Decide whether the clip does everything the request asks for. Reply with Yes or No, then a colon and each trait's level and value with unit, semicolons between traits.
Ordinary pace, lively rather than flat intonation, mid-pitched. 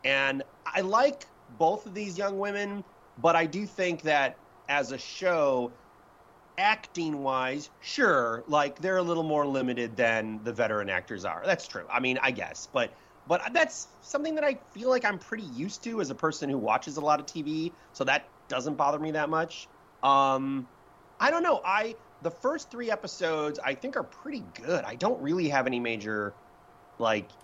Yes: average, 185 wpm; wide, 6.9 semitones; medium, 155 Hz